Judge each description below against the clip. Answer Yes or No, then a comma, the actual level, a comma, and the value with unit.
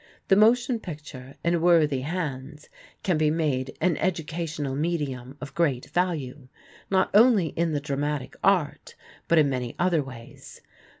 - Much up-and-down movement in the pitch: No, average, 4.0 semitones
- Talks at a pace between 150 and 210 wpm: No, average, 140 wpm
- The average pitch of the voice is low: No, medium, 155 Hz